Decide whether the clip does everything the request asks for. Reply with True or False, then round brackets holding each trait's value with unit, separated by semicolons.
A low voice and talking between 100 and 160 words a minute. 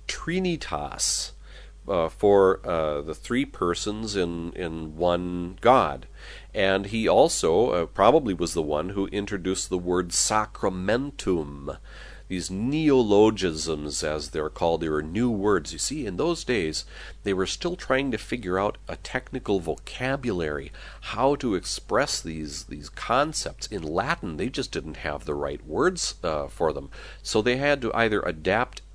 True (95 Hz; 150 wpm)